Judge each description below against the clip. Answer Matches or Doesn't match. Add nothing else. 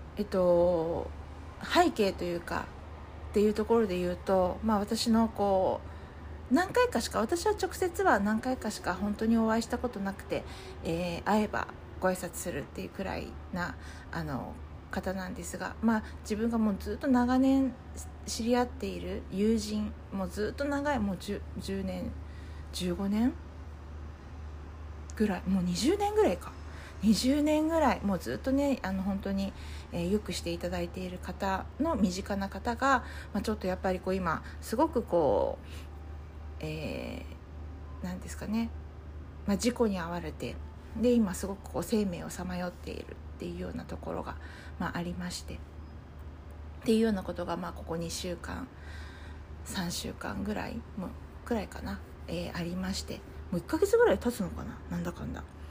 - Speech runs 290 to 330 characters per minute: Matches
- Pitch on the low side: Doesn't match